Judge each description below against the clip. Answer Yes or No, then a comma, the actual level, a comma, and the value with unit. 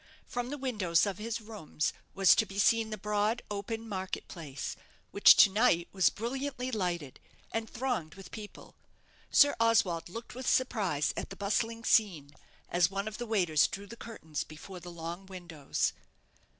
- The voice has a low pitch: No, high, 200 Hz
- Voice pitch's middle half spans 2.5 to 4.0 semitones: No, average, 4.6 semitones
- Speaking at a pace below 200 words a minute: Yes, average, 165 wpm